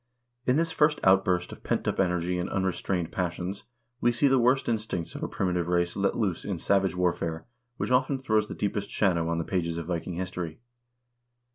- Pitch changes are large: No, average, 3.6 semitones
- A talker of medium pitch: No, very low, 95 Hz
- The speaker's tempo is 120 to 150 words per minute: No, average, 190 wpm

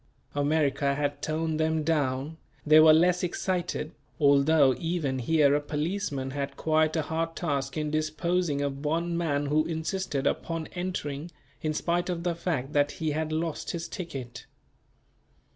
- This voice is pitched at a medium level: Yes, medium, 155 Hz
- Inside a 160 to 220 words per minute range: No, average, 150 wpm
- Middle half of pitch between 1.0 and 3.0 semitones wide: Yes, narrow, 2.6 semitones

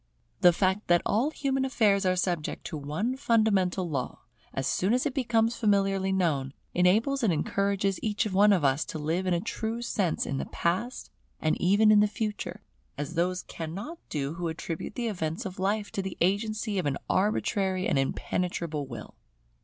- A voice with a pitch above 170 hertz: Yes, high, 190 Hz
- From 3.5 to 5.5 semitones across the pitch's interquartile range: Yes, average, 4.3 semitones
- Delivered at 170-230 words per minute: Yes, average, 180 wpm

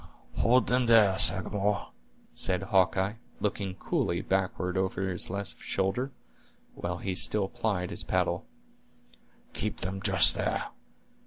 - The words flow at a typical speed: No, slow, 120 wpm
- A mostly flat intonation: Yes, narrow, 1.9 semitones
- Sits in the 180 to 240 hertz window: No, very low, 95 Hz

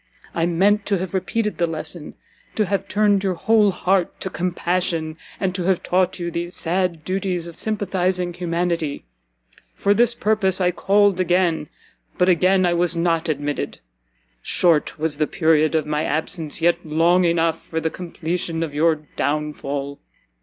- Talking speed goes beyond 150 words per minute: Yes, average, 160 wpm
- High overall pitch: No, medium, 175 Hz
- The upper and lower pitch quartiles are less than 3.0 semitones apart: Yes, narrow, 2.6 semitones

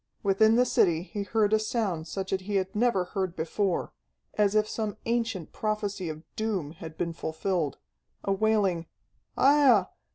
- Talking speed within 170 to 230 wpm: No, average, 160 wpm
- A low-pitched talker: No, high, 195 Hz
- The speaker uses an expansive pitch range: No, average, 3.7 semitones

